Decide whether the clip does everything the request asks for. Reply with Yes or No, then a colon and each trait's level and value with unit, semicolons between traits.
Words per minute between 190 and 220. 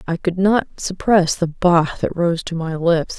Yes: fast, 205 wpm